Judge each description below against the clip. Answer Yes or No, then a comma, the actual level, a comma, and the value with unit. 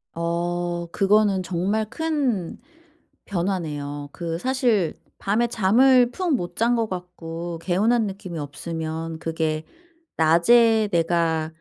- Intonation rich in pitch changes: No, average, 4.9 semitones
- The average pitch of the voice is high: No, medium, 180 Hz